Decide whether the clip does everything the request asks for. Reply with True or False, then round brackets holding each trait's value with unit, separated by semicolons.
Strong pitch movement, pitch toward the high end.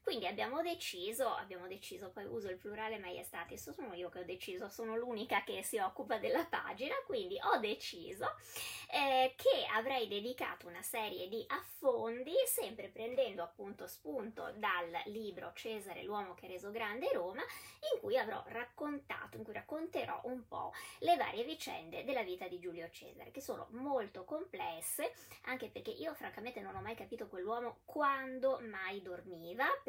True (8.6 semitones; 240 Hz)